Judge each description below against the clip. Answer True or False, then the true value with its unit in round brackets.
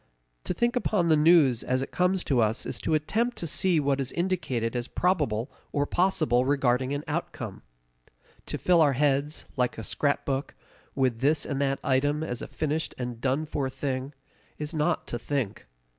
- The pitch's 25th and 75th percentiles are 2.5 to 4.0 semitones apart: True (3.7 semitones)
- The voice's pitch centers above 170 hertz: False (145 Hz)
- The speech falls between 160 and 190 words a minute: True (180 wpm)